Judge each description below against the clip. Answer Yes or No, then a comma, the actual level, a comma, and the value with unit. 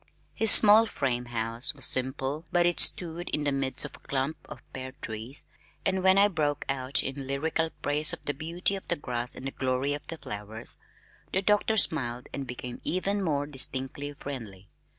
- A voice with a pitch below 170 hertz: Yes, medium, 140 Hz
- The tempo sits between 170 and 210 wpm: Yes, average, 185 wpm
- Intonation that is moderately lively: Yes, average, 4.5 semitones